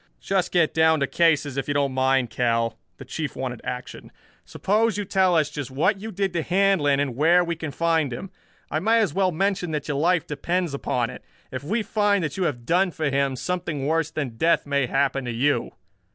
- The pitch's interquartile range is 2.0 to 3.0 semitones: No, average, 4.8 semitones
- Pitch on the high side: No, medium, 155 Hz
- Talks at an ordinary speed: No, fast, 215 wpm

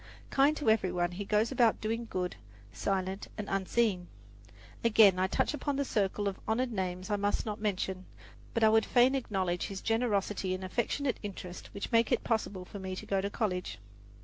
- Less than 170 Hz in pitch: No, high, 205 Hz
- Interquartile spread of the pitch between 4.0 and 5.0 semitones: No, average, 3.4 semitones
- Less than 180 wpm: No, average, 190 wpm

